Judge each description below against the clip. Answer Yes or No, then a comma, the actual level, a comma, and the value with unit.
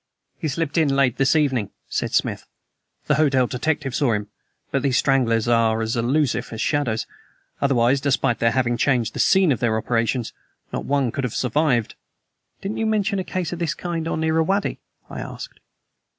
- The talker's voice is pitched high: No, low, 135 Hz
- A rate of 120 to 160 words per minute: No, average, 180 wpm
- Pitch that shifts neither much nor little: Yes, average, 5.0 semitones